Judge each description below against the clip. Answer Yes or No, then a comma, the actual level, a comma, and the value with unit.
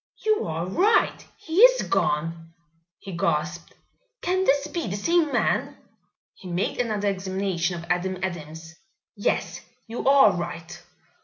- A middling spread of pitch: No, wide, 8.3 semitones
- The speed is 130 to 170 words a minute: Yes, slow, 135 wpm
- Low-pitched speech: No, high, 190 Hz